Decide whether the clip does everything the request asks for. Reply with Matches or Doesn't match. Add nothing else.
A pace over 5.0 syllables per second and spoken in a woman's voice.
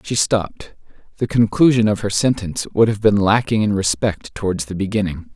Doesn't match